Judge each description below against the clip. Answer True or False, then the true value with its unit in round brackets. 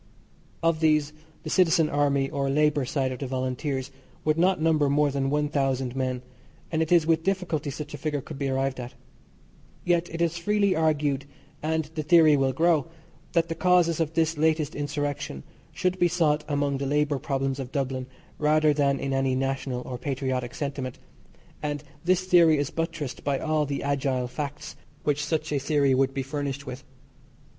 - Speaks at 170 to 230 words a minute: True (180 wpm)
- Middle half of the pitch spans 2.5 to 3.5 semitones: True (2.8 semitones)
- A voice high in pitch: False (145 Hz)